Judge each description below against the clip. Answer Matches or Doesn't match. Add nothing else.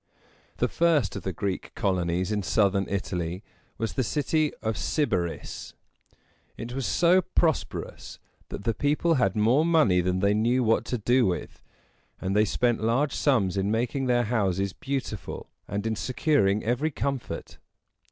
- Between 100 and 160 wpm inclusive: Matches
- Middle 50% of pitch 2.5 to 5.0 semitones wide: Doesn't match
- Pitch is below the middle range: Matches